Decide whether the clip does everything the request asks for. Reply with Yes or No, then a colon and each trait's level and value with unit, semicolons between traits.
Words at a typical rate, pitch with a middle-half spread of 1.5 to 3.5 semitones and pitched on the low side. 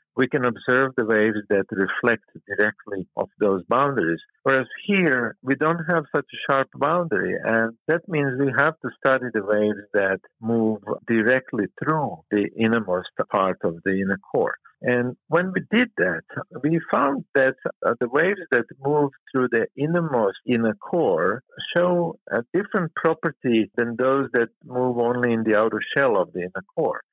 No: average, 165 wpm; average, 5.1 semitones; low, 125 Hz